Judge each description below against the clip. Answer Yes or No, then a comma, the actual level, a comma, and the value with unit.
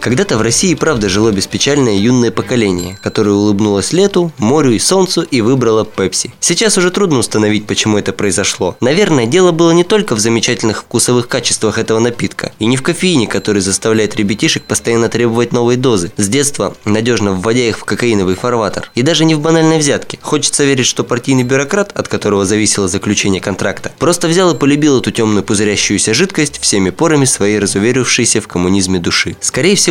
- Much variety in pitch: Yes, wide, 5.8 semitones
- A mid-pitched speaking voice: No, low, 115 Hz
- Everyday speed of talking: No, fast, 175 wpm